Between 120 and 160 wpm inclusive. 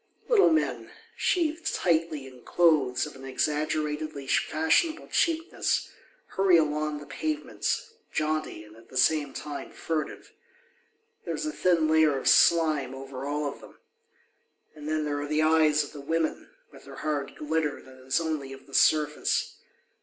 Yes: average, 155 wpm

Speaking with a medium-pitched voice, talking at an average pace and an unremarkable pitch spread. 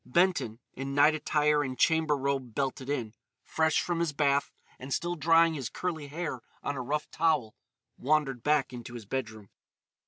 Yes: medium, 145 Hz; average, 165 wpm; average, 3.5 semitones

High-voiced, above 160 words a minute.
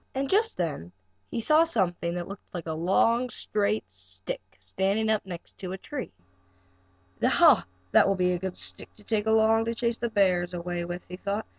Yes: high, 195 Hz; average, 175 wpm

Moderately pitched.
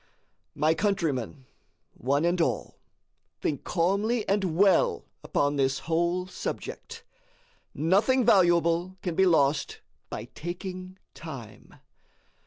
Yes: medium, 175 Hz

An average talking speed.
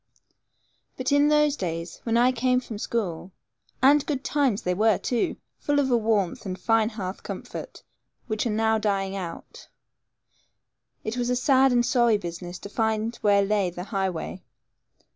Yes: average, 160 wpm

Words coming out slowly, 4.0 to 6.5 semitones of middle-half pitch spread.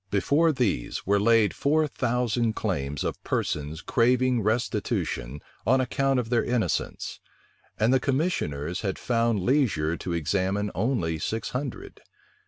Yes: slow, 130 wpm; wide, 5.5 semitones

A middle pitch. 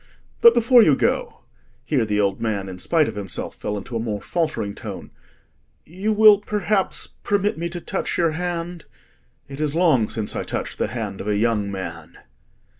Yes: medium, 150 Hz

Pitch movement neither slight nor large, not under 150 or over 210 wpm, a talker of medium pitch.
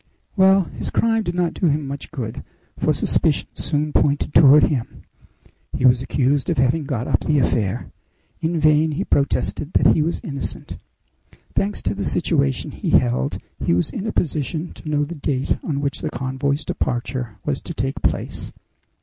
Yes: average, 3.5 semitones; average, 175 wpm; medium, 145 Hz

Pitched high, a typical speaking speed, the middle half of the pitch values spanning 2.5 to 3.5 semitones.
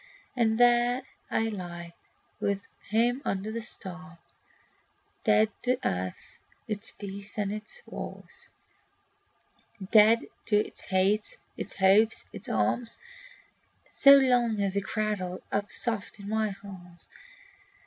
No: high, 210 Hz; slow, 120 wpm; average, 3.0 semitones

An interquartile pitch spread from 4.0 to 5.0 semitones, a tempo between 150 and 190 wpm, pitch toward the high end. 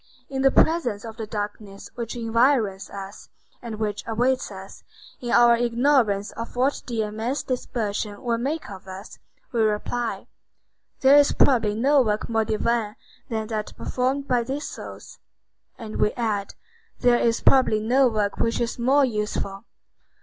No: average, 2.9 semitones; average, 155 wpm; high, 230 Hz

